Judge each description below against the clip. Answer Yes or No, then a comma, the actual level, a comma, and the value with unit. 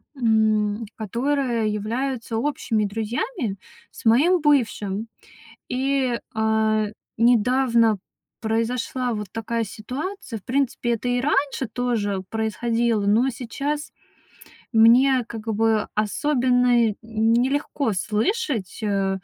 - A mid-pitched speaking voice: No, high, 230 Hz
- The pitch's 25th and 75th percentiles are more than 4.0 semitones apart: No, average, 3.1 semitones